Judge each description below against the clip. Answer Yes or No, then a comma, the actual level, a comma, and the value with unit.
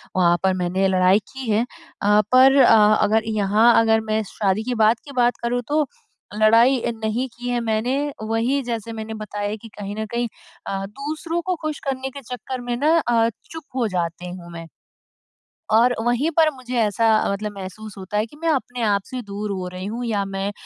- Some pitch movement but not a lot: Yes, average, 3.5 semitones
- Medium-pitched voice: No, high, 225 Hz